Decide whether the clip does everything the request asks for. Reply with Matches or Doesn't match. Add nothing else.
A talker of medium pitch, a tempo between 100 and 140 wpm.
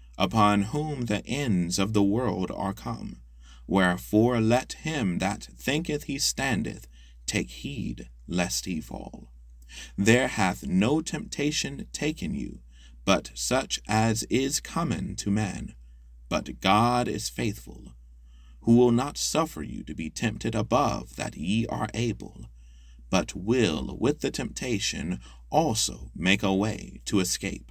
Doesn't match